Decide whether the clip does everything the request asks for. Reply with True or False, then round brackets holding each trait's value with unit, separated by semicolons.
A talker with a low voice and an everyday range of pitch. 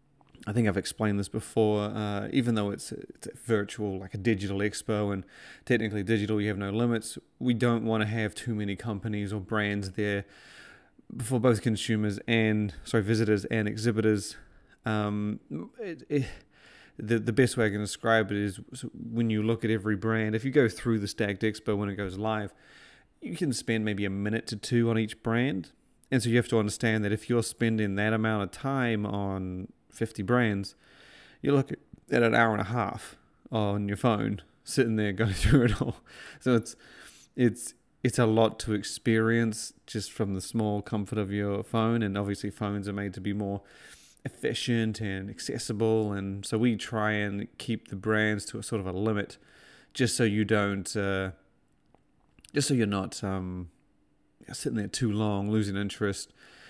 False (110 Hz; 2.1 semitones)